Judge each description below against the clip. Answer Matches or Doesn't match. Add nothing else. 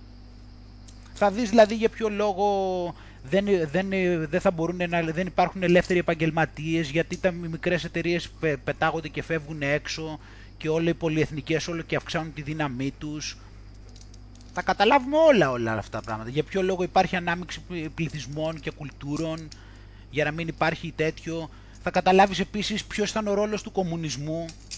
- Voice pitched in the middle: Matches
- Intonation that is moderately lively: Matches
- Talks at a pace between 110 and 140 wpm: Doesn't match